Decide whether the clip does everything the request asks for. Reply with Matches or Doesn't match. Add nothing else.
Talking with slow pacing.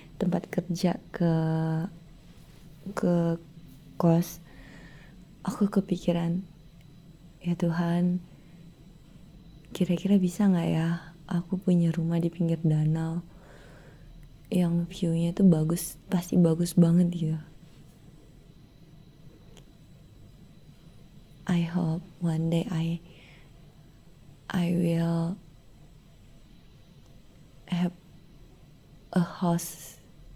Matches